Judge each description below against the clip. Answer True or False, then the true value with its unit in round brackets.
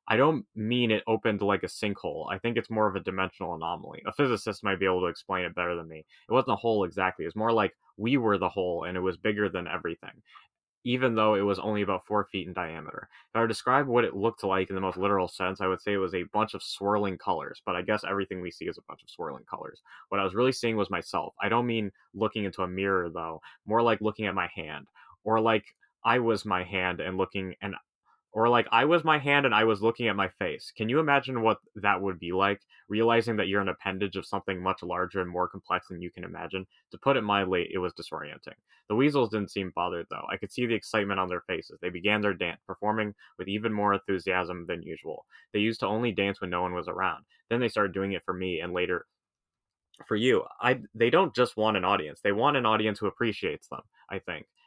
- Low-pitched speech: True (100 Hz)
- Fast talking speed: True (250 wpm)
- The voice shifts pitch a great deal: False (2.9 semitones)